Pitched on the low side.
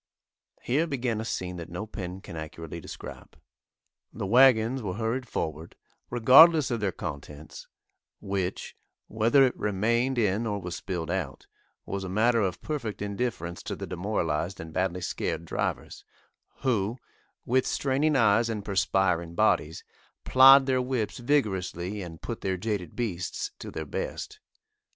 Yes: low, 105 Hz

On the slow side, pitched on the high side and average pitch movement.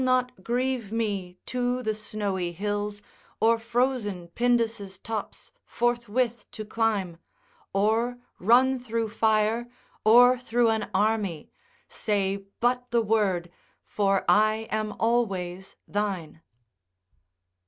Yes: slow, 110 wpm; high, 220 Hz; average, 3.1 semitones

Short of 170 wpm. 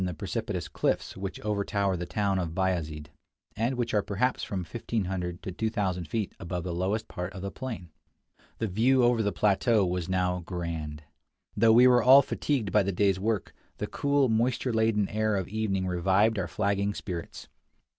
No: average, 175 wpm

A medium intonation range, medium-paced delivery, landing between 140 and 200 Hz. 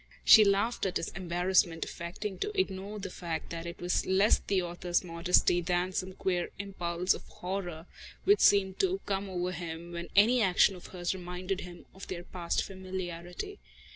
No: narrow, 1.9 semitones; average, 170 wpm; medium, 185 Hz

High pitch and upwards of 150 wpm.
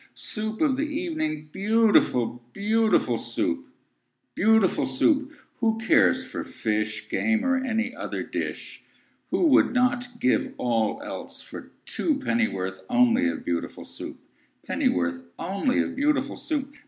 No: high, 225 Hz; average, 140 wpm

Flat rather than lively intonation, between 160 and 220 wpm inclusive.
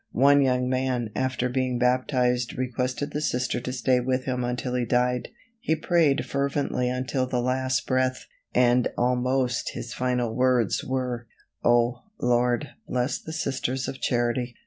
No: narrow, 1.1 semitones; average, 145 wpm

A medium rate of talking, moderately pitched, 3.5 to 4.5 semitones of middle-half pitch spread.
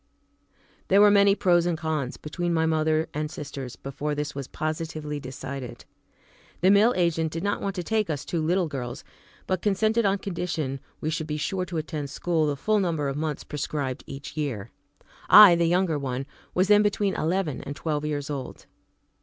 Yes: average, 185 wpm; medium, 160 Hz; average, 4.0 semitones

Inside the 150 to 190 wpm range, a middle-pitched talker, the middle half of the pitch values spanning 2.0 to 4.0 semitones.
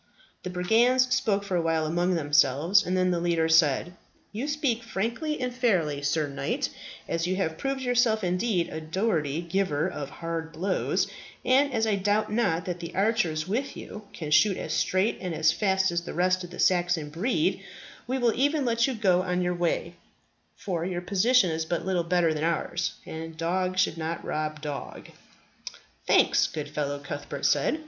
No: average, 185 wpm; medium, 180 Hz; average, 4.9 semitones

